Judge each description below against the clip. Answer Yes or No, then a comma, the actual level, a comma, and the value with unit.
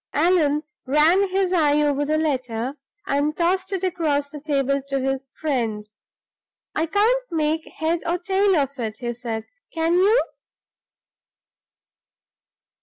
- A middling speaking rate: No, slow, 130 wpm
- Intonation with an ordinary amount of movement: Yes, average, 4.4 semitones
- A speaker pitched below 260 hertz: No, very high, 300 Hz